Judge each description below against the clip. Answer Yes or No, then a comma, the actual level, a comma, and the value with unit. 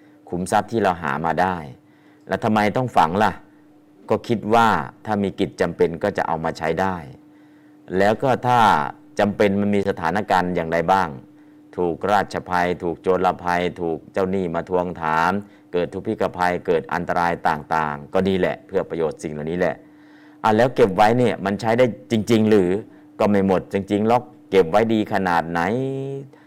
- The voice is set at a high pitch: No, low, 100 Hz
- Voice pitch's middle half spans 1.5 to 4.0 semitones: No, average, 4.4 semitones